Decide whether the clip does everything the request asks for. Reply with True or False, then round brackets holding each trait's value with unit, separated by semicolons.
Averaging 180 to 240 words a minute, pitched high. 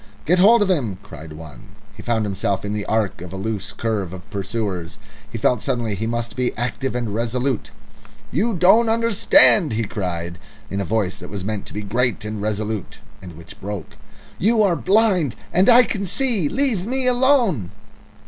False (185 wpm; 110 Hz)